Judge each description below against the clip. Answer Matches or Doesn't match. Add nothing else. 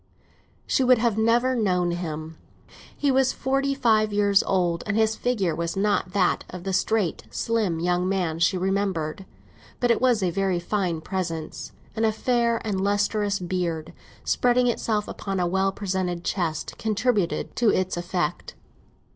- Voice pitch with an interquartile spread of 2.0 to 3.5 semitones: Doesn't match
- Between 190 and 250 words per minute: Doesn't match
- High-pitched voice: Matches